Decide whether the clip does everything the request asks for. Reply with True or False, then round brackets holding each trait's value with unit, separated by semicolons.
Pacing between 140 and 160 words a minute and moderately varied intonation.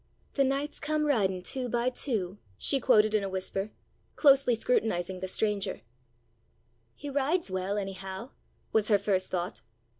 False (145 wpm; 6.0 semitones)